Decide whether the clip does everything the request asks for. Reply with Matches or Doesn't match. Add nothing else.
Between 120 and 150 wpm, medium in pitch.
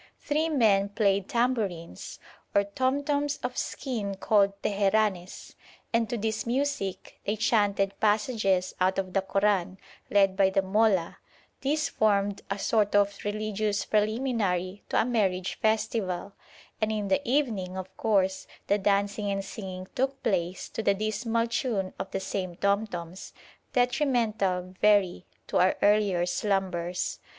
Doesn't match